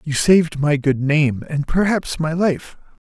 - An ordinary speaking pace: Yes, average, 175 wpm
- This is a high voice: No, medium, 155 Hz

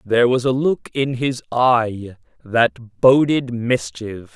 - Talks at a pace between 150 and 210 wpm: No, average, 140 wpm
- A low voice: Yes, low, 120 Hz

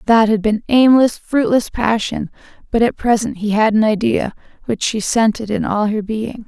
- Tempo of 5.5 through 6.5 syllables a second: No, 4.7 syllables/s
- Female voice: Yes, female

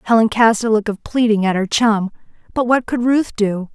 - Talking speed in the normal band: No, fast, 225 wpm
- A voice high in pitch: Yes, high, 220 Hz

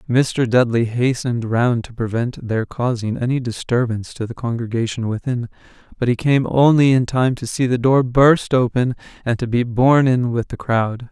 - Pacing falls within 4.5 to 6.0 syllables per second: Yes, 4.9 syllables/s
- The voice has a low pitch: Yes, low, 120 Hz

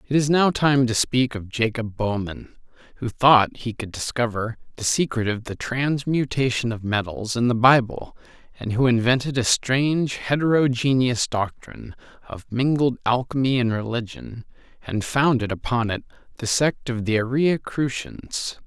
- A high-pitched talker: No, low, 120 Hz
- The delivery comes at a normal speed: Yes, average, 150 wpm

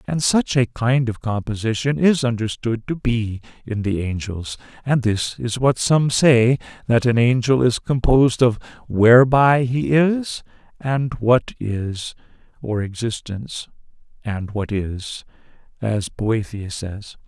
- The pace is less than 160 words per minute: Yes, slow, 135 wpm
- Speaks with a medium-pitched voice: No, low, 120 Hz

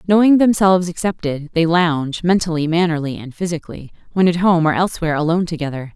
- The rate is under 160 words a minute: Yes, average, 140 wpm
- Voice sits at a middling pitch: Yes, medium, 170 Hz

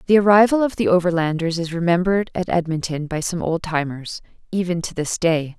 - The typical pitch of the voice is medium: Yes, medium, 175 Hz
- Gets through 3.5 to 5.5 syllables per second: No, 5.7 syllables/s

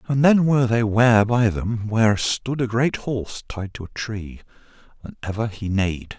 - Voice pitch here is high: No, low, 110 Hz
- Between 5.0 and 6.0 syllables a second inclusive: No, 4.7 syllables/s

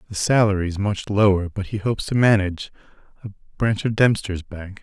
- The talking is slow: No, average, 160 wpm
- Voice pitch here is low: Yes, low, 100 Hz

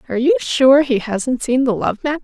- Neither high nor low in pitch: No, very high, 265 Hz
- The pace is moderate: No, fast, 240 wpm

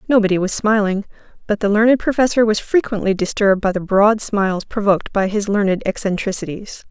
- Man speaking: No, female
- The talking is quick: No, average, 165 wpm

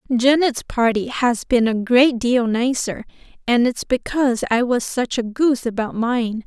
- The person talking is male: No, female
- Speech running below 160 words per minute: No, average, 165 wpm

